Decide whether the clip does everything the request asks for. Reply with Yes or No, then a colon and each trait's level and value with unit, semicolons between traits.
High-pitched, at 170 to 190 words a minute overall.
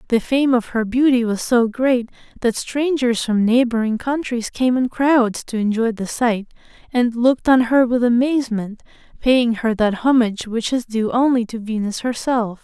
Yes: high, 240 Hz; average, 175 wpm